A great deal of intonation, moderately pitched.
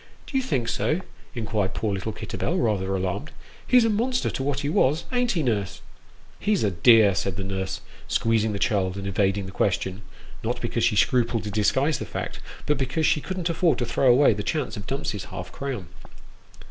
No: wide, 6.6 semitones; low, 115 Hz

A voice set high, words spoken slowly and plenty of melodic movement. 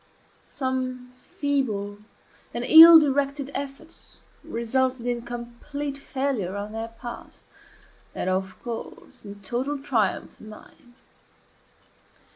No: very high, 250 Hz; slow, 100 wpm; average, 3.8 semitones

